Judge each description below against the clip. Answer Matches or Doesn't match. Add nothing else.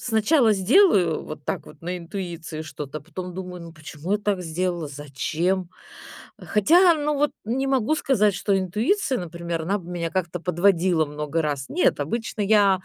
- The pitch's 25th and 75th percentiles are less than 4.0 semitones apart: Doesn't match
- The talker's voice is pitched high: Doesn't match